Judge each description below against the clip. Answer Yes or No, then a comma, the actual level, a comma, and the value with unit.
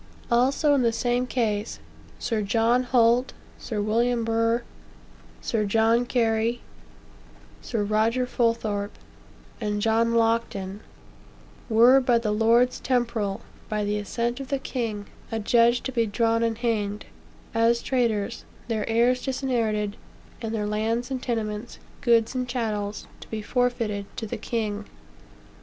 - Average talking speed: No, slow, 130 wpm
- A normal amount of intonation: No, narrow, 2.3 semitones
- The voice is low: No, high, 230 Hz